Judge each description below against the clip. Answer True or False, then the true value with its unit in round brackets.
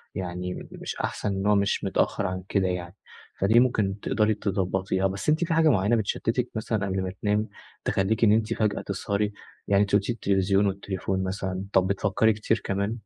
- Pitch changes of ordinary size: False (2.1 semitones)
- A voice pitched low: True (100 Hz)